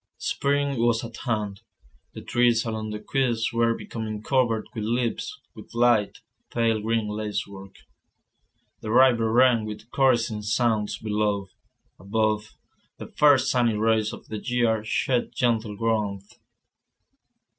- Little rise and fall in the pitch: Yes, narrow, 2.0 semitones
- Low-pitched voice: Yes, low, 115 Hz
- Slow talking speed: Yes, slow, 125 wpm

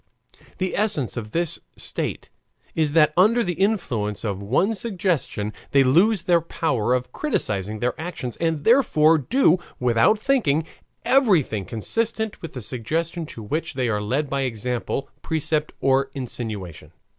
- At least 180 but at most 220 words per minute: No, average, 145 wpm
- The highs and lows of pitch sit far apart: Yes, wide, 6.9 semitones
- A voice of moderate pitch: Yes, medium, 150 Hz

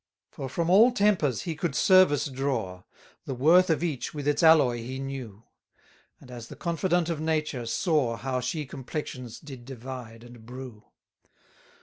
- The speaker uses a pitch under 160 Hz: Yes, low, 135 Hz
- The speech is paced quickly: No, average, 160 wpm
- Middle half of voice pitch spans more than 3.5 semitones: Yes, average, 4.7 semitones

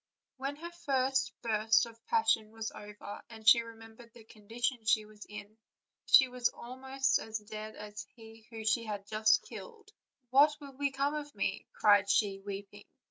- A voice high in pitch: Yes, high, 225 Hz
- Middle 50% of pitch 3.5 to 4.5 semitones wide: Yes, average, 3.8 semitones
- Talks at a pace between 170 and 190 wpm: Yes, average, 175 wpm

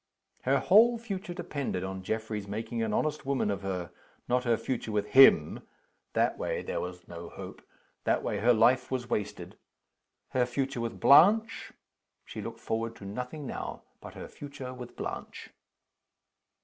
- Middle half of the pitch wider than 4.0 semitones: Yes, average, 4.8 semitones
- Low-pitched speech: Yes, low, 120 Hz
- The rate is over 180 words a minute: No, average, 160 wpm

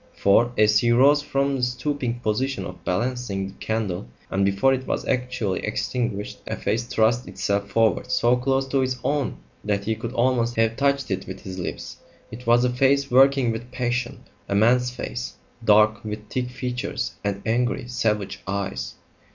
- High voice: No, low, 120 Hz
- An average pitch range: Yes, average, 3.2 semitones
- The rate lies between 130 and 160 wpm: No, average, 175 wpm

